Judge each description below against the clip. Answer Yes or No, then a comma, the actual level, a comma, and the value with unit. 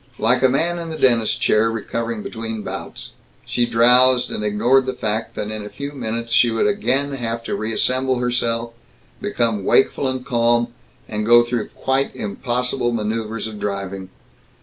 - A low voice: Yes, low, 115 Hz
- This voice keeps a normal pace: Yes, average, 165 wpm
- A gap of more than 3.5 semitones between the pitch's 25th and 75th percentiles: No, narrow, 2.6 semitones